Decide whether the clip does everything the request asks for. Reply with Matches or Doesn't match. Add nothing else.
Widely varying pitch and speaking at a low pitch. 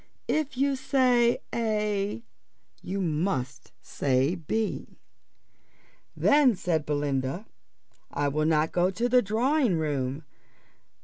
Doesn't match